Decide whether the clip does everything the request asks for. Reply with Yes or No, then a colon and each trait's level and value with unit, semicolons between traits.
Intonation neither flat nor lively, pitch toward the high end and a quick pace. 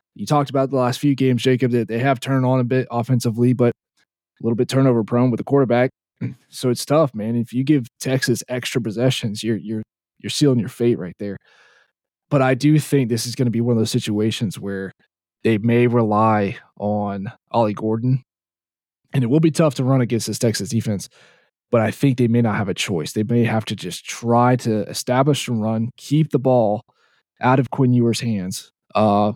No: average, 3.0 semitones; low, 120 Hz; fast, 210 wpm